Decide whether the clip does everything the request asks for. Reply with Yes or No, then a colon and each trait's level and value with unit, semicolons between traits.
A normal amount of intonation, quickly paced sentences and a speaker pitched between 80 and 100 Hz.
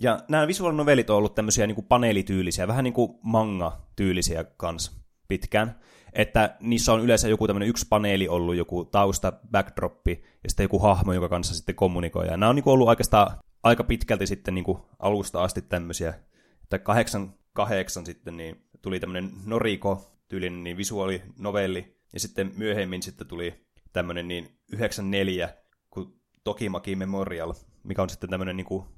Yes: average, 3.0 semitones; fast, 165 wpm; very low, 95 Hz